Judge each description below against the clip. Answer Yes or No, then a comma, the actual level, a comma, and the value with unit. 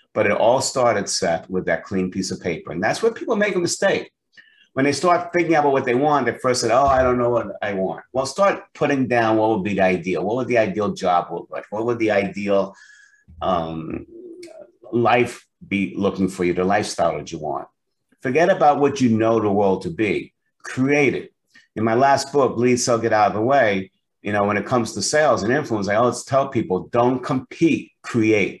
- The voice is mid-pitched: No, low, 120 Hz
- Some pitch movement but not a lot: No, wide, 6.2 semitones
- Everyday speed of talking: No, fast, 220 wpm